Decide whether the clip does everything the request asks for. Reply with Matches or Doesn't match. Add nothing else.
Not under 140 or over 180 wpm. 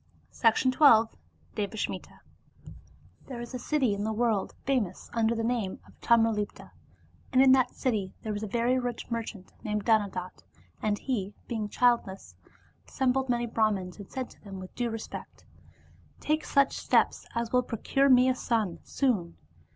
Matches